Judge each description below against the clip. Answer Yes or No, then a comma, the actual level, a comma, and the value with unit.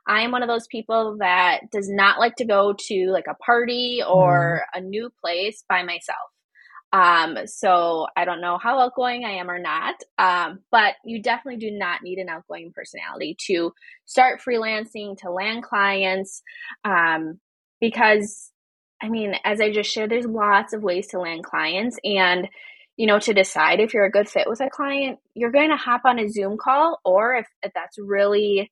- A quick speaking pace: No, average, 190 wpm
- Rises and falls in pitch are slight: No, average, 4.2 semitones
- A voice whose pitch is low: No, high, 210 Hz